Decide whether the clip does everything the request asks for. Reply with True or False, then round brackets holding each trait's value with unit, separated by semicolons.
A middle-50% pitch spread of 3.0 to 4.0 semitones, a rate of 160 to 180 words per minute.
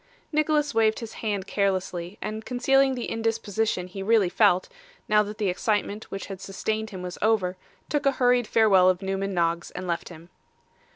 True (3.4 semitones; 175 wpm)